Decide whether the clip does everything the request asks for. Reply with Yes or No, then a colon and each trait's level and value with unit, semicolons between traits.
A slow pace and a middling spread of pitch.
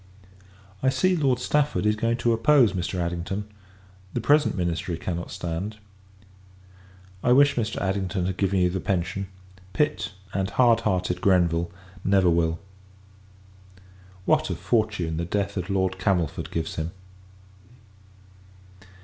Yes: slow, 130 wpm; average, 4.7 semitones